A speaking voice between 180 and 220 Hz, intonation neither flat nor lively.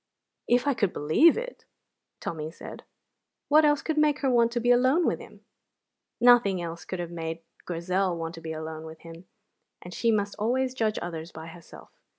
No: high, 190 Hz; wide, 7.1 semitones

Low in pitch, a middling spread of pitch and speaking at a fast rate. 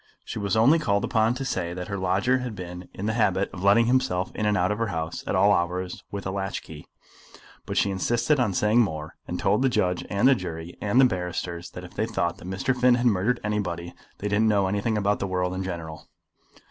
Yes: low, 100 Hz; average, 3.7 semitones; fast, 235 wpm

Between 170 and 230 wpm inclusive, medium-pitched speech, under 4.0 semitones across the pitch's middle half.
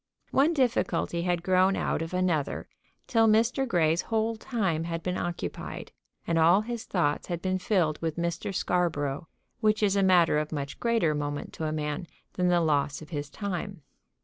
No: average, 175 wpm; medium, 175 Hz; average, 4.3 semitones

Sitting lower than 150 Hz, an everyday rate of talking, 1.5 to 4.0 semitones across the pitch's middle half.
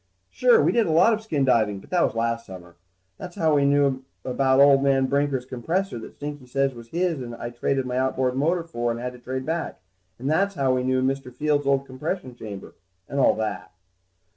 No: low, 135 Hz; fast, 225 wpm; average, 3.1 semitones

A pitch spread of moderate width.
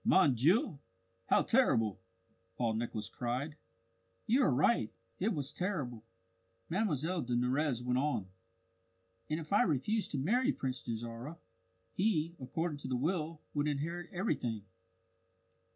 No: wide, 6.1 semitones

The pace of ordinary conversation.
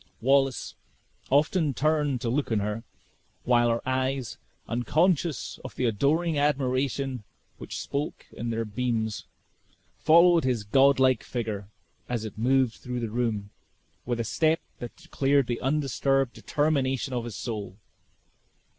No: slow, 130 wpm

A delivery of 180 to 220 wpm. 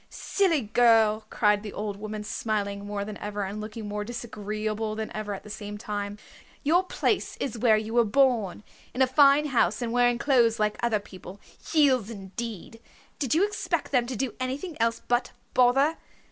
Yes: average, 185 wpm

